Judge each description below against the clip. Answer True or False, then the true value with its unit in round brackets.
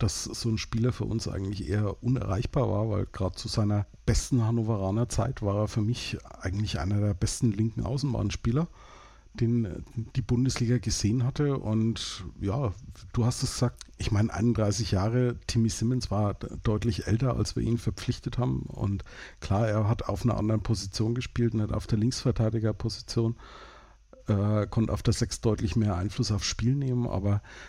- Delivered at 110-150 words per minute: False (170 wpm)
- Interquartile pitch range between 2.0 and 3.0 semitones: True (2.5 semitones)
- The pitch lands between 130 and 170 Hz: False (110 Hz)